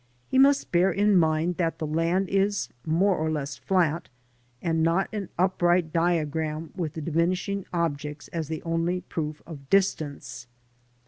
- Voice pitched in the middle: Yes, medium, 165 Hz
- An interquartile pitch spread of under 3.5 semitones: Yes, average, 2.8 semitones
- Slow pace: No, average, 150 wpm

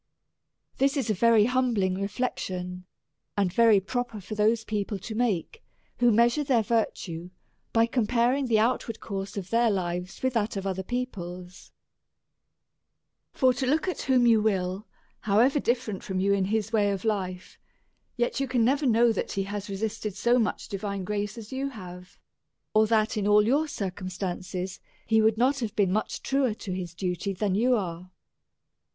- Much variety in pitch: No, average, 3.8 semitones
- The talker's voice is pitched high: Yes, high, 215 Hz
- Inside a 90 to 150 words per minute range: No, average, 175 wpm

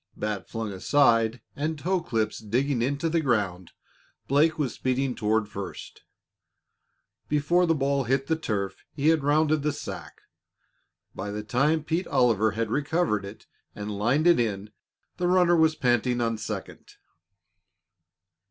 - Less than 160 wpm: Yes, average, 145 wpm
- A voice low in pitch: Yes, low, 130 Hz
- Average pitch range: No, wide, 6.3 semitones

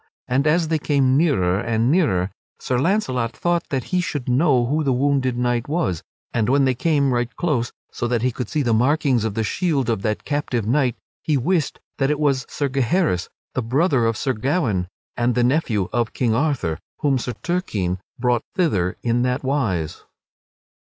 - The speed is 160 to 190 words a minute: Yes, average, 185 wpm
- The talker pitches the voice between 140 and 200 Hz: No, low, 130 Hz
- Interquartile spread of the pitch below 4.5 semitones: Yes, average, 4.1 semitones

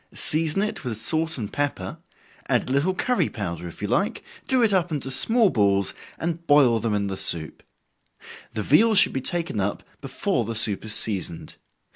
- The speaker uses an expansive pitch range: Yes, wide, 8.5 semitones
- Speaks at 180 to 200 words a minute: Yes, average, 185 wpm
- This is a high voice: No, low, 130 Hz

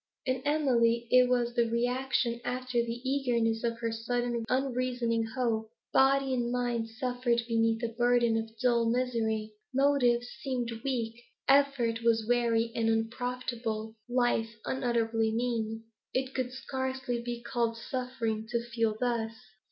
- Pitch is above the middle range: Yes, high, 240 Hz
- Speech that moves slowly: Yes, slow, 130 wpm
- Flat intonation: Yes, narrow, 1.7 semitones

